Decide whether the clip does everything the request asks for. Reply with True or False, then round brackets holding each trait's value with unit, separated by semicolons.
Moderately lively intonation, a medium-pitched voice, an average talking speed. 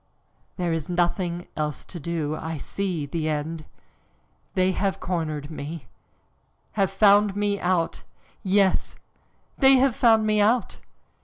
False (4.1 semitones; 180 Hz; 130 wpm)